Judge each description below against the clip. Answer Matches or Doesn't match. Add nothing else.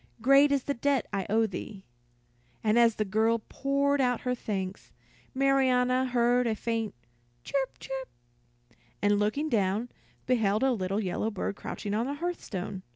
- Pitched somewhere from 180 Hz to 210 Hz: Doesn't match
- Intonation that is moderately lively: Matches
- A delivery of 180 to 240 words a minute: Doesn't match